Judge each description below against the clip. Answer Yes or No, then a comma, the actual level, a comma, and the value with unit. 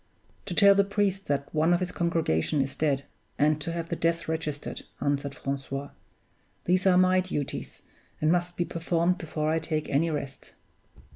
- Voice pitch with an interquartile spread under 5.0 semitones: Yes, average, 3.6 semitones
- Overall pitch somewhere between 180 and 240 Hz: No, medium, 165 Hz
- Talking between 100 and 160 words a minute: No, average, 170 wpm